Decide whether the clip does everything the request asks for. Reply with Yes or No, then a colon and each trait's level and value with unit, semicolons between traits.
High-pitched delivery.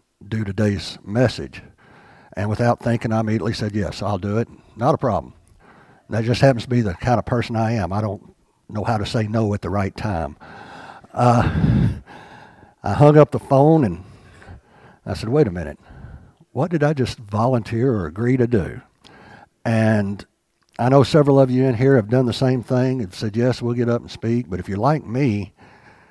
No: low, 115 Hz